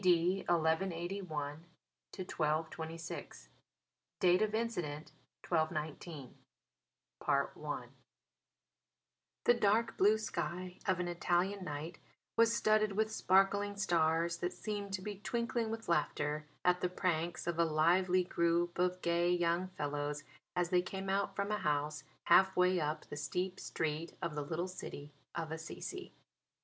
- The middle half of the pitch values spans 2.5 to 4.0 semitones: Yes, average, 3.3 semitones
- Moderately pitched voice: Yes, medium, 175 Hz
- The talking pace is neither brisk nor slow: No, slow, 130 wpm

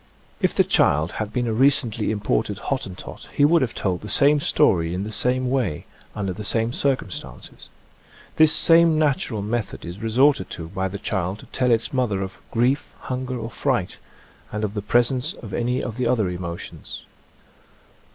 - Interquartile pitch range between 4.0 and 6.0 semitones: Yes, average, 4.5 semitones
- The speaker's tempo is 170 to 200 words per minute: Yes, average, 180 wpm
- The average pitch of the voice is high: No, low, 115 Hz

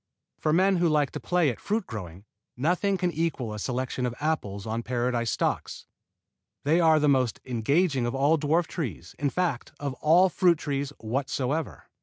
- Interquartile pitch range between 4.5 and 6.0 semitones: Yes, average, 5.3 semitones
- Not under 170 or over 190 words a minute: Yes, average, 180 wpm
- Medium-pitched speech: Yes, medium, 145 Hz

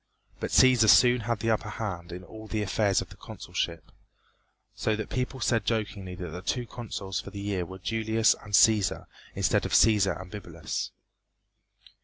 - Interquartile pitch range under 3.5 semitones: Yes, average, 3.1 semitones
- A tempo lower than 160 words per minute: No, average, 180 wpm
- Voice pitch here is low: Yes, low, 105 Hz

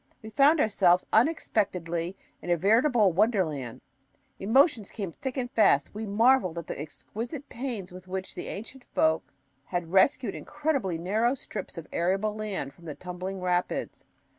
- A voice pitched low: No, high, 195 Hz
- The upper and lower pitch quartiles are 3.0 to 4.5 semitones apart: No, average, 5.1 semitones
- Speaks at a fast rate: No, average, 150 wpm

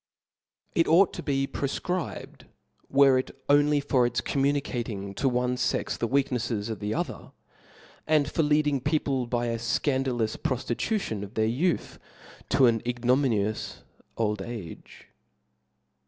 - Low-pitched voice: Yes, low, 125 Hz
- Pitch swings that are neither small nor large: Yes, average, 3.7 semitones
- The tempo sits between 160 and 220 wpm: No, slow, 135 wpm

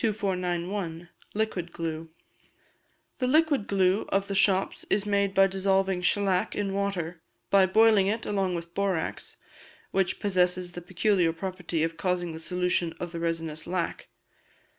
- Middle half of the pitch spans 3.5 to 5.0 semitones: No, narrow, 2.4 semitones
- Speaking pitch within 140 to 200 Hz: Yes, medium, 185 Hz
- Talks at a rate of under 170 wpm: Yes, average, 140 wpm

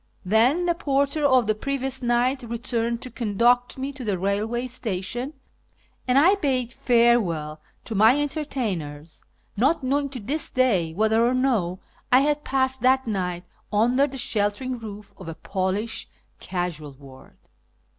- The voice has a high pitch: Yes, high, 240 Hz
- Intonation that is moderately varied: Yes, average, 4.7 semitones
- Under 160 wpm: Yes, average, 145 wpm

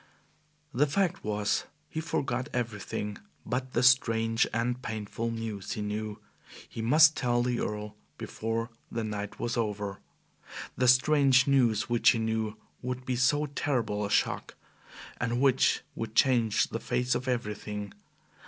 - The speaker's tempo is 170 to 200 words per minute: No, average, 145 wpm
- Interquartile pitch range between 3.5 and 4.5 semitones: No, average, 2.9 semitones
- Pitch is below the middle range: Yes, low, 115 Hz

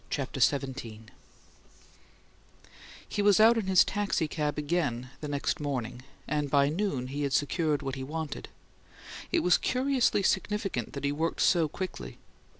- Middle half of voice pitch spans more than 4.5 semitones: Yes, average, 5.3 semitones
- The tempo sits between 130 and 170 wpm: Yes, average, 145 wpm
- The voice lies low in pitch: No, medium, 150 Hz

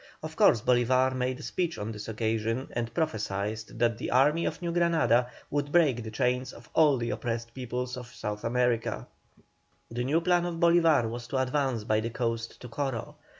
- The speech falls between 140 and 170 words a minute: No, average, 190 wpm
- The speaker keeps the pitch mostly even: No, average, 3.9 semitones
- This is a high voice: No, low, 125 Hz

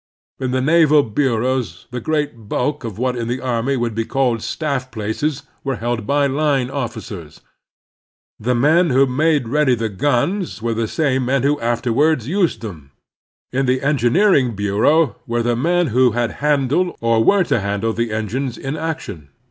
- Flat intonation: No, average, 4.1 semitones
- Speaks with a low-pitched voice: Yes, low, 130 Hz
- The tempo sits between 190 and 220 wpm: No, average, 175 wpm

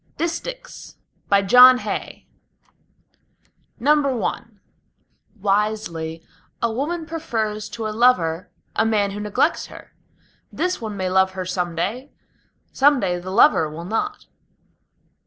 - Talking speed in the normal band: No, slow, 120 wpm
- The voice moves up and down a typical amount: No, wide, 5.8 semitones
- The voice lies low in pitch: No, high, 215 Hz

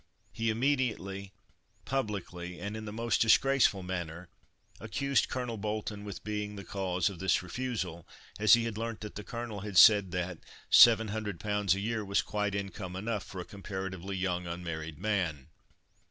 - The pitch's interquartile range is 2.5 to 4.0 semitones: Yes, average, 3.0 semitones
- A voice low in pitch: Yes, low, 100 Hz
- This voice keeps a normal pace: Yes, average, 160 wpm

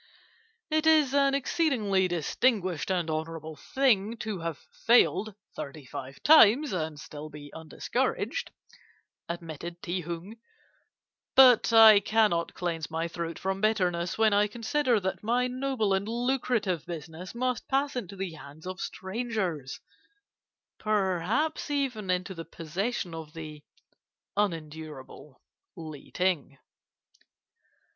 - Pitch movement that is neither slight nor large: No, wide, 6.1 semitones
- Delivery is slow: Yes, slow, 120 wpm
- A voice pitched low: No, high, 190 Hz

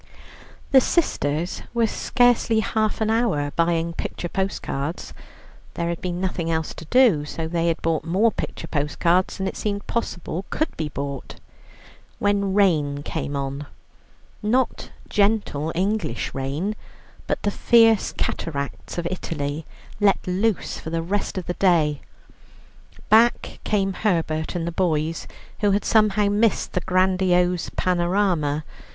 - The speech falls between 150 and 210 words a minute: No, slow, 135 wpm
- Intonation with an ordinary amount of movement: Yes, average, 4.3 semitones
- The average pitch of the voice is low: No, medium, 180 Hz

